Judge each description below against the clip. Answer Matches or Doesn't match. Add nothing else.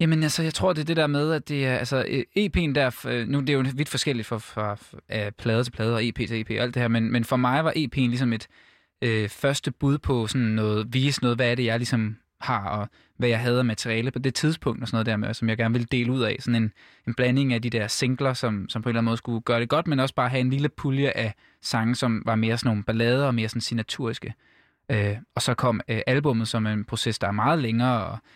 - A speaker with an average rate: Doesn't match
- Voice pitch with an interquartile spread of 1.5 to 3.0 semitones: Matches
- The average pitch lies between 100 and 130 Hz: Matches